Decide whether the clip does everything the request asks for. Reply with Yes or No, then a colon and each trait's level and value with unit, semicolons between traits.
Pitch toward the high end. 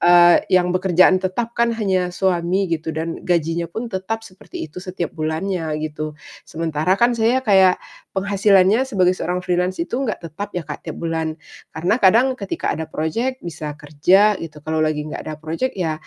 No: medium, 180 Hz